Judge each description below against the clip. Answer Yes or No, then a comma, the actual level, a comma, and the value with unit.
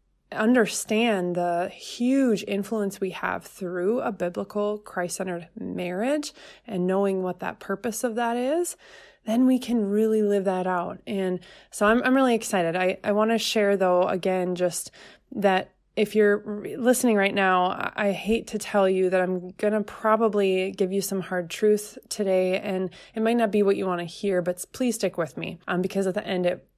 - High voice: Yes, high, 200 Hz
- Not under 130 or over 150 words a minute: No, average, 190 wpm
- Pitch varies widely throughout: No, average, 3.1 semitones